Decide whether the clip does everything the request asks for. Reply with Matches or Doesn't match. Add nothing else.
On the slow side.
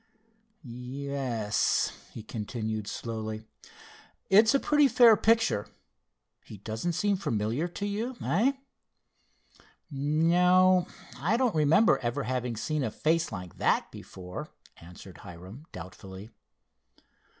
Matches